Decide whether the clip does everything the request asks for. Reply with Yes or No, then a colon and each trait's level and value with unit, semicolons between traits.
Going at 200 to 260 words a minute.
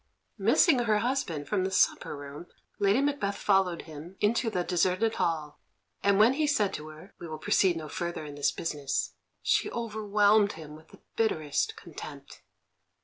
No: average, 165 wpm